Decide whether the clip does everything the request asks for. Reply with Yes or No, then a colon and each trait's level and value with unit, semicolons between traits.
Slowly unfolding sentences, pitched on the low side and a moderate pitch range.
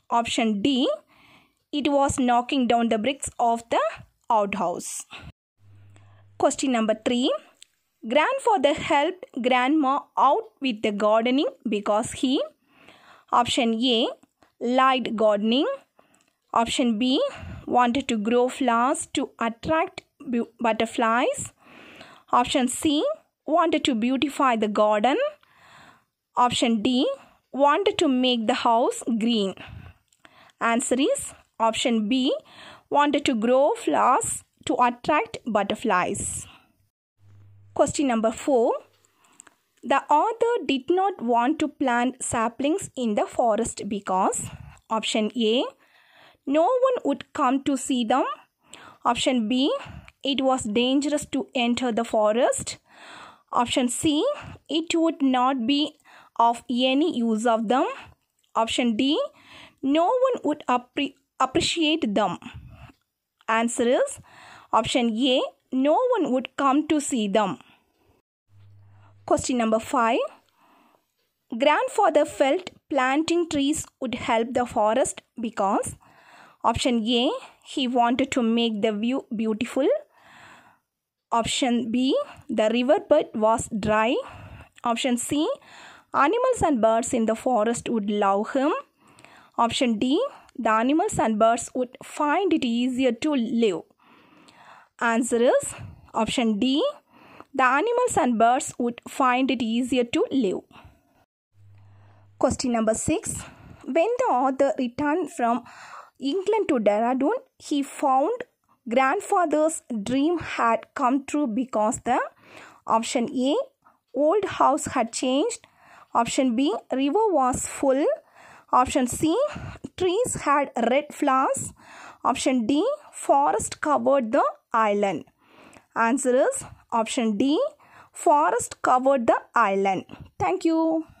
No: slow, 110 wpm; very high, 260 Hz; average, 4.2 semitones